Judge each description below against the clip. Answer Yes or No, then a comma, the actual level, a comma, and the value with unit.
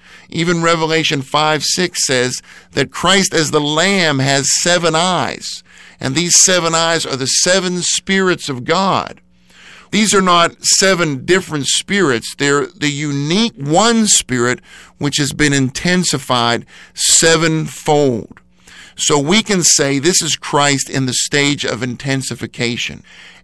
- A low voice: No, medium, 155 Hz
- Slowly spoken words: Yes, slow, 130 wpm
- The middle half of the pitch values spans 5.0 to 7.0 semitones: No, average, 4.5 semitones